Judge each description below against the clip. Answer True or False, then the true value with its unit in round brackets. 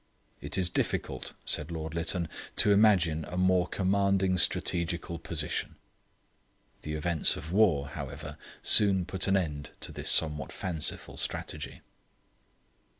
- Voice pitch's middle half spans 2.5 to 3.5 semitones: True (3.1 semitones)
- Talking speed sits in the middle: False (130 wpm)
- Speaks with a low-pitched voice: True (85 Hz)